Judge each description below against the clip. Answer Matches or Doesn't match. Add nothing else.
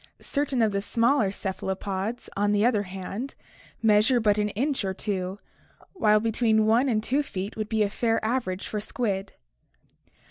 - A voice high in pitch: Matches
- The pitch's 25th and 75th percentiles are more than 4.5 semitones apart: Doesn't match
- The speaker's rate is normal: Matches